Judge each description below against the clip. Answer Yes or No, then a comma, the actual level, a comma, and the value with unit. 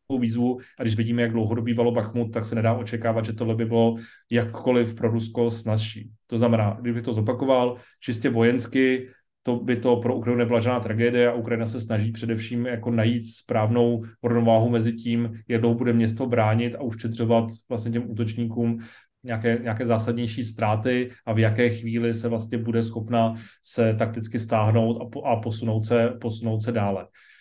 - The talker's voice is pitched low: Yes, low, 115 Hz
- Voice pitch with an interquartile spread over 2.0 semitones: No, narrow, 0.9 semitones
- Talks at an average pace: No, fast, 170 wpm